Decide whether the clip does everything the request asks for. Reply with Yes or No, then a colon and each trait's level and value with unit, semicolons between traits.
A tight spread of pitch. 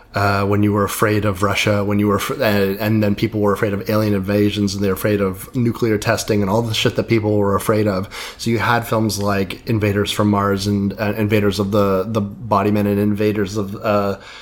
Yes: narrow, 1.3 semitones